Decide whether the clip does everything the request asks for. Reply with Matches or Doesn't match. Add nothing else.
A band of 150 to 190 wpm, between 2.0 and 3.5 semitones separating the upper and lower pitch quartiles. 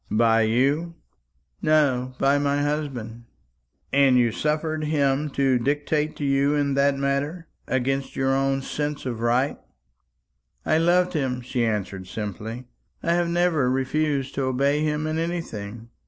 Doesn't match